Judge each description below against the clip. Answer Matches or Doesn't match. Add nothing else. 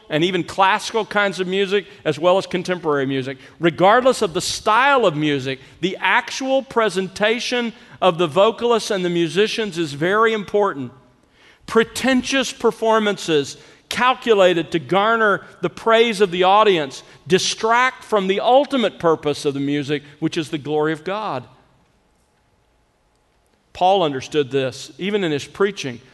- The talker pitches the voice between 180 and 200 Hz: Matches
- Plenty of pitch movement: Matches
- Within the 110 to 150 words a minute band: Matches